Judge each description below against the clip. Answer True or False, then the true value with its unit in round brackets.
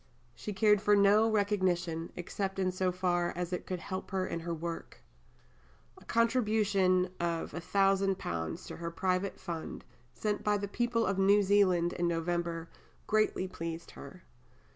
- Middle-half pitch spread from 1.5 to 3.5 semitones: True (2.9 semitones)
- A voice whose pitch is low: False (185 Hz)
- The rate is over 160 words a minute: False (150 wpm)